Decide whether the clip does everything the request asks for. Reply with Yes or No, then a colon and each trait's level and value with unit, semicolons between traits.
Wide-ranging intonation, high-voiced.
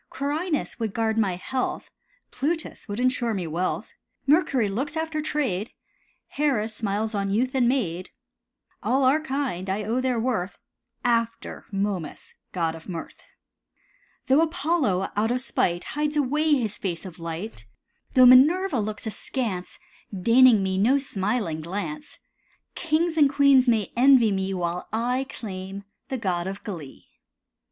Yes: wide, 5.9 semitones; high, 230 Hz